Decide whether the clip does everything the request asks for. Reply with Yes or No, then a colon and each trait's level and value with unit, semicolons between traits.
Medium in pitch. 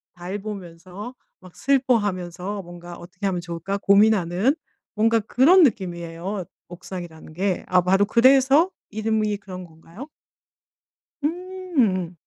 No: high, 195 Hz